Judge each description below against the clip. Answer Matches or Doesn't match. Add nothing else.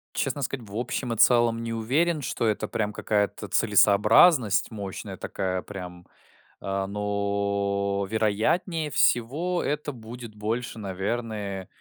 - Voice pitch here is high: Doesn't match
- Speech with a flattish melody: Doesn't match